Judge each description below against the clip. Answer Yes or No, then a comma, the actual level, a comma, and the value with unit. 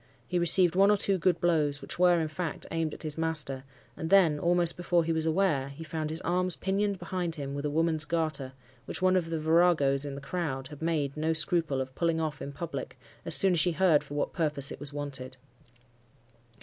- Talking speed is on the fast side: Yes, fast, 220 wpm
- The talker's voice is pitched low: No, medium, 160 Hz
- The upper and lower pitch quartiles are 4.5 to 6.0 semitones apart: No, average, 3.2 semitones